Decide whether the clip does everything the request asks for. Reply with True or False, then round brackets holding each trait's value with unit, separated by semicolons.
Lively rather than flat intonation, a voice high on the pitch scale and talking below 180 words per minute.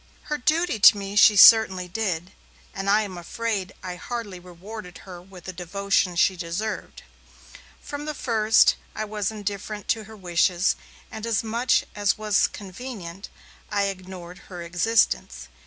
False (3.3 semitones; 200 Hz; 150 wpm)